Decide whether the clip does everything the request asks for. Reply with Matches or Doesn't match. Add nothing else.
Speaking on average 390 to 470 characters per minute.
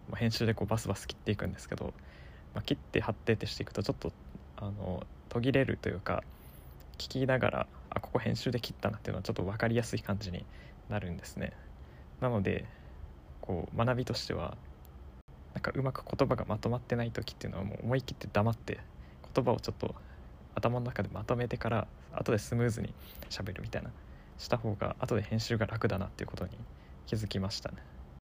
Matches